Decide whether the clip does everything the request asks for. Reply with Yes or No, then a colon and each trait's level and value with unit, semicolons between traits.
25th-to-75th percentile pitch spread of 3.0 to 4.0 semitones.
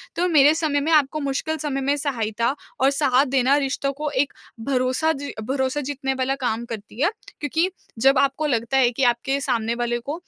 No: narrow, 2.5 semitones